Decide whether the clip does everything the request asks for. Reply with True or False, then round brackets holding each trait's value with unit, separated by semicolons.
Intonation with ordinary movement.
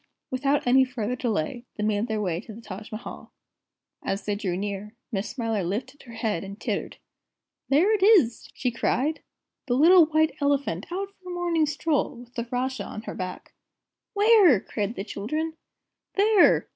False (6.8 semitones)